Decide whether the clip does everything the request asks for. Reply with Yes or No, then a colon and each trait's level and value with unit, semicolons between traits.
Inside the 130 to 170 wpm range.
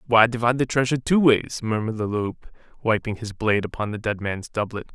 No: fast, 205 wpm